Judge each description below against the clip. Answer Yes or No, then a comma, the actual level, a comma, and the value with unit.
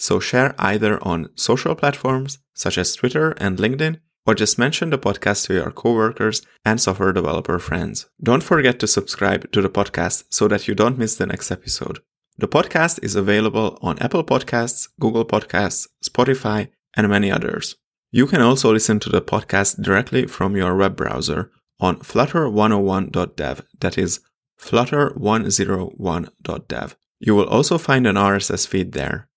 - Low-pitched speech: Yes, low, 110 Hz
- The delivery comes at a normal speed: Yes, average, 155 wpm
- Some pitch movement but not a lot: Yes, average, 3.7 semitones